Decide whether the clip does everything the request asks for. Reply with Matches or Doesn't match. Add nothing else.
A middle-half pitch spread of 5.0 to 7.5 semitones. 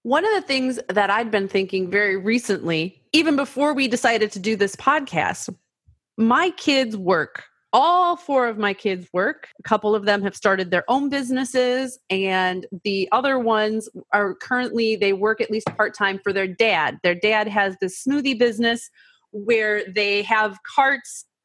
Doesn't match